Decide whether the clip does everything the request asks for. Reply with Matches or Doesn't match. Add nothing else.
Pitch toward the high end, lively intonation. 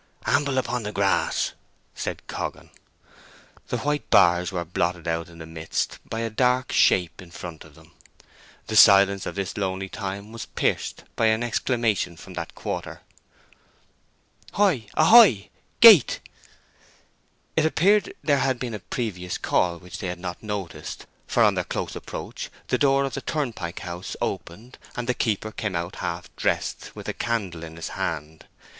Doesn't match